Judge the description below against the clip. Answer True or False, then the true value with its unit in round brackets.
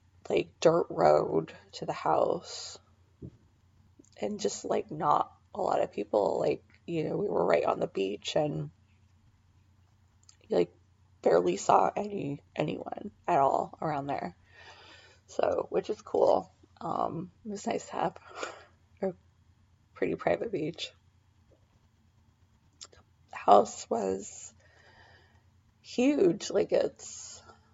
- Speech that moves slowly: True (115 wpm)